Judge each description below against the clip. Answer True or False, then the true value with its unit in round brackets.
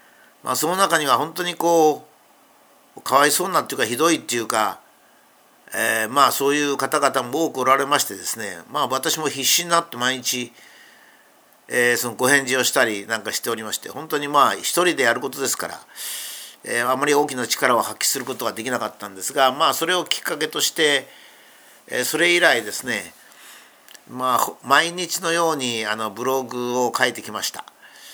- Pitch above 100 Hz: True (135 Hz)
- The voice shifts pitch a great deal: False (4.2 semitones)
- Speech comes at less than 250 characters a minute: False (335 characters per minute)